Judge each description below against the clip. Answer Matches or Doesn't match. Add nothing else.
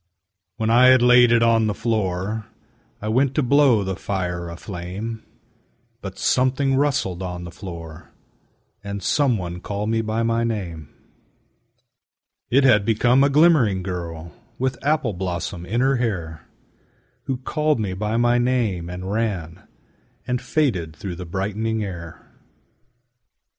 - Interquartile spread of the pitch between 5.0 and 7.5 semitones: Matches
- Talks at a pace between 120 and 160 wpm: Matches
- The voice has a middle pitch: Doesn't match